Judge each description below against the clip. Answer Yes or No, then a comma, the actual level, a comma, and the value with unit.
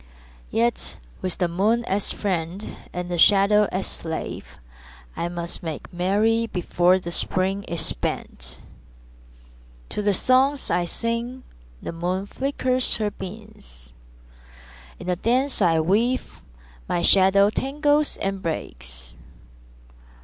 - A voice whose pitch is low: No, high, 190 Hz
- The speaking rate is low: Yes, slow, 120 wpm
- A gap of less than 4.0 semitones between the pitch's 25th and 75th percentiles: No, average, 4.8 semitones